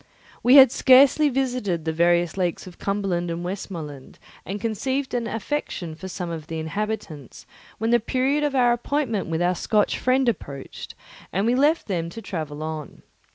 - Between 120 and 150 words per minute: No, average, 170 wpm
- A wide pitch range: Yes, wide, 6.9 semitones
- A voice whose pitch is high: Yes, high, 200 Hz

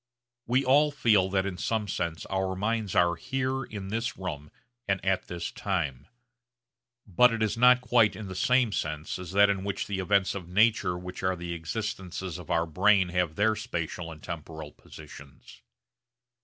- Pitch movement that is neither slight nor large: Yes, average, 4.1 semitones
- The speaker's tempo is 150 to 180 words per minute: Yes, average, 175 wpm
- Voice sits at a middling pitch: No, very low, 95 Hz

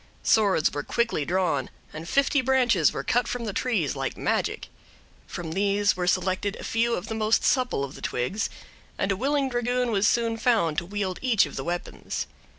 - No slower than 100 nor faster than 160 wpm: No, average, 190 wpm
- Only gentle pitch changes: No, average, 5.2 semitones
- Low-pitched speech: No, high, 205 Hz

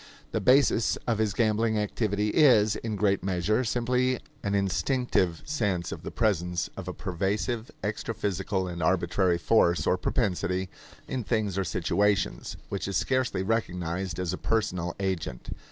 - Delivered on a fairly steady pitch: No, average, 3.7 semitones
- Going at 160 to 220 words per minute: No, average, 145 wpm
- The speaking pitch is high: No, low, 100 Hz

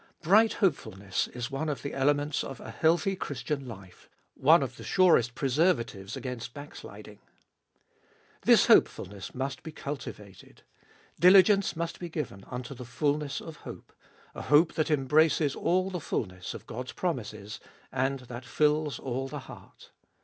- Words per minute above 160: No, average, 155 wpm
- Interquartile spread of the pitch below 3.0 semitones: No, average, 4.8 semitones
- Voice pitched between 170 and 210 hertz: No, medium, 140 Hz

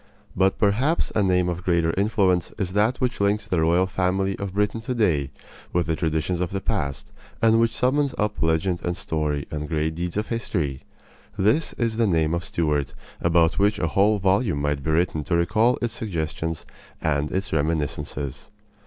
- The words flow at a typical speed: Yes, average, 180 wpm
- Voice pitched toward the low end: Yes, very low, 90 Hz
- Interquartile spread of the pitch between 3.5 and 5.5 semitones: Yes, average, 4.7 semitones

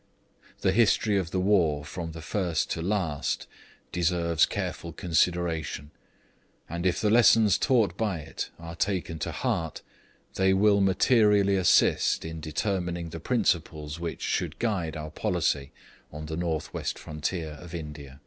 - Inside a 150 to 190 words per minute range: No, average, 140 wpm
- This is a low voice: Yes, very low, 85 Hz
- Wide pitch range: No, average, 3.5 semitones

